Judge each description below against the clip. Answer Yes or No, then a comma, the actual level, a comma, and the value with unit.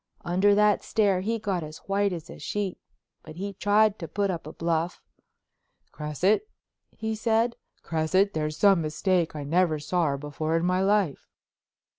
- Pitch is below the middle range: No, medium, 185 Hz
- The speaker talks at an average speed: Yes, average, 165 wpm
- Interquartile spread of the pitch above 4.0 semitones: Yes, average, 4.4 semitones